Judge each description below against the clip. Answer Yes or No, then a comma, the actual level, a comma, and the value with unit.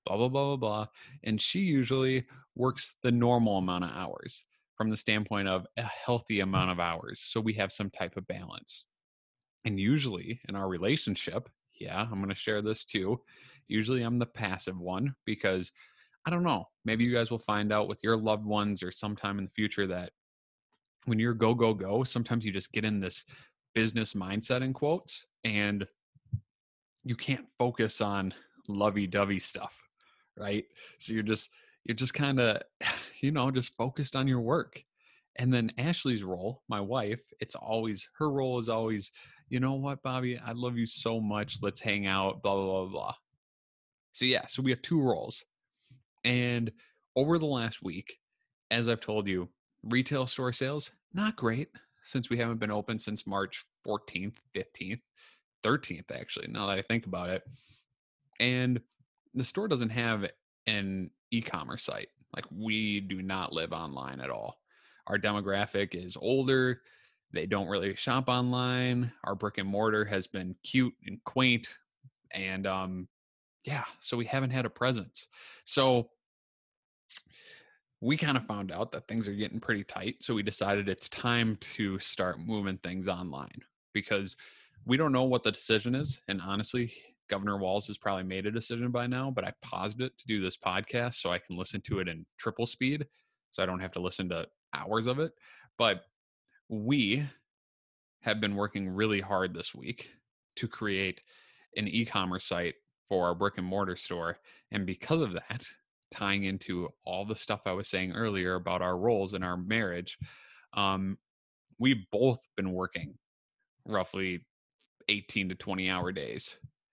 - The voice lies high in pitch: No, low, 110 Hz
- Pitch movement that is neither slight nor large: Yes, average, 4.2 semitones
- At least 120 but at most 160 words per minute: No, average, 170 wpm